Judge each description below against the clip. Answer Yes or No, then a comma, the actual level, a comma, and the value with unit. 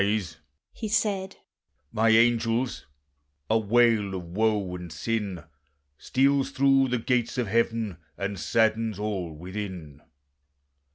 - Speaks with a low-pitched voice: Yes, low, 110 Hz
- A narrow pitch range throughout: No, average, 3.9 semitones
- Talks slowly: Yes, slow, 115 wpm